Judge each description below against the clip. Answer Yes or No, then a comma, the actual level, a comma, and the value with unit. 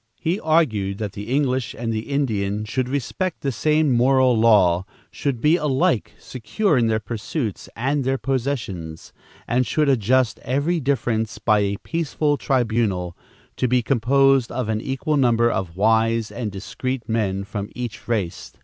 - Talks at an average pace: Yes, average, 155 wpm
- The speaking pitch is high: No, low, 120 Hz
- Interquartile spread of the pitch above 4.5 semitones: No, average, 4.2 semitones